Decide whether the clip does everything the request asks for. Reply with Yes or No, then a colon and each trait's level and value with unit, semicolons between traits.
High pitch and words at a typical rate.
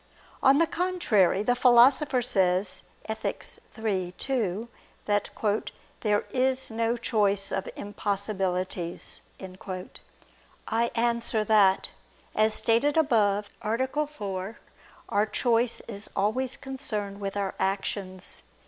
No: high, 215 Hz; slow, 105 wpm